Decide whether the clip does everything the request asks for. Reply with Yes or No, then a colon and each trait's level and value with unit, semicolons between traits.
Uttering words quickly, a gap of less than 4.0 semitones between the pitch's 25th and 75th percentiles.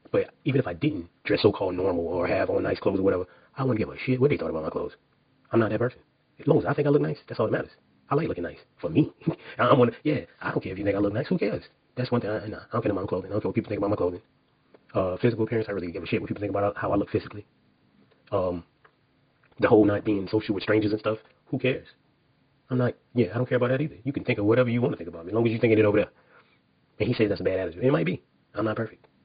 Yes: fast, 315 wpm; average, 3.6 semitones